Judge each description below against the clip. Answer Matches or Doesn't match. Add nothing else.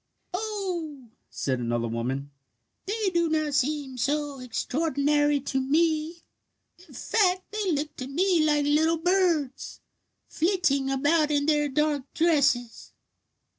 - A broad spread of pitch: Doesn't match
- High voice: Matches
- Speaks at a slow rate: Matches